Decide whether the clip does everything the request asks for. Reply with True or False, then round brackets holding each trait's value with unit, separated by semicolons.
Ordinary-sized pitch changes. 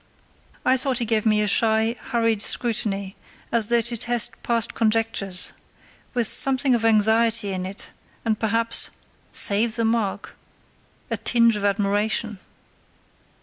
False (1.9 semitones)